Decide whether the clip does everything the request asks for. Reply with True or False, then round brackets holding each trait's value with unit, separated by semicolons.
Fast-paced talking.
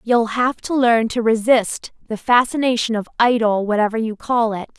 False (175 wpm)